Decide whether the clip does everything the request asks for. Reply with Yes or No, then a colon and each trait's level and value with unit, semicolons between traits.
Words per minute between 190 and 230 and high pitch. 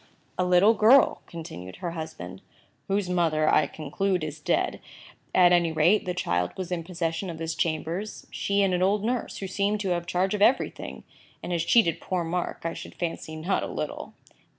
No: average, 195 wpm; medium, 175 Hz